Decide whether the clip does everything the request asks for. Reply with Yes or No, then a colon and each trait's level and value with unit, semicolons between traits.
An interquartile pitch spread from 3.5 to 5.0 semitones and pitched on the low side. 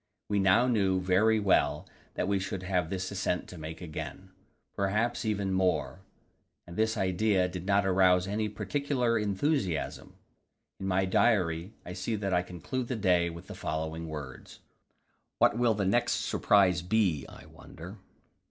No: average, 2.9 semitones; very low, 95 Hz